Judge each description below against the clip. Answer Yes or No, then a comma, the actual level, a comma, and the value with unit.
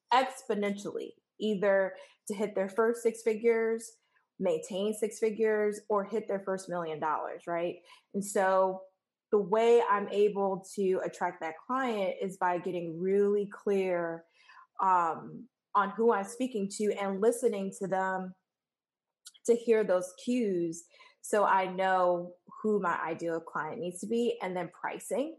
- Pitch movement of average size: Yes, average, 3.4 semitones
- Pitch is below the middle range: No, high, 205 Hz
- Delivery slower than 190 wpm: Yes, average, 140 wpm